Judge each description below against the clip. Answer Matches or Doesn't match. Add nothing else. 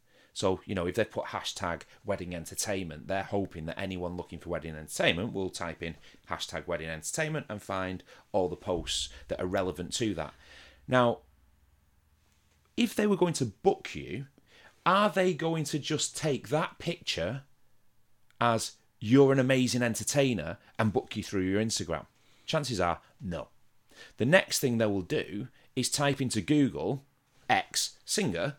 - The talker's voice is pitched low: Matches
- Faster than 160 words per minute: Doesn't match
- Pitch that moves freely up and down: Matches